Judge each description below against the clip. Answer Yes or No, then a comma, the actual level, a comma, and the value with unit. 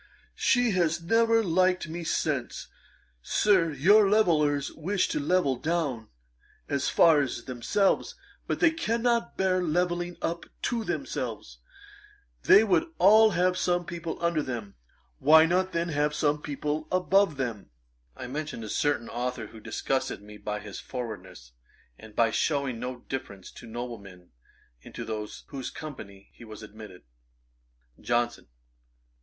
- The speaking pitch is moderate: Yes, medium, 150 Hz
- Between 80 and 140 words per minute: Yes, slow, 135 wpm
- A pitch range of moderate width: No, wide, 7.3 semitones